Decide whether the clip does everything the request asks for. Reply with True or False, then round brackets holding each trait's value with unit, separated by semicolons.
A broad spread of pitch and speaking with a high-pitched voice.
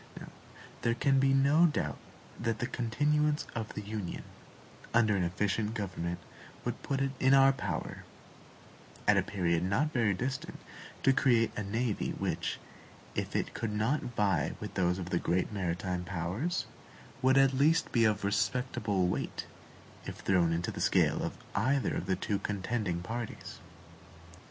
False (6.0 semitones; 110 Hz)